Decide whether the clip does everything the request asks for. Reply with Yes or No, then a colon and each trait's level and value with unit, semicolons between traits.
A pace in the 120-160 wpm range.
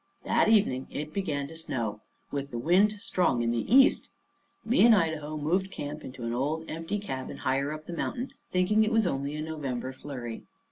No: average, 190 wpm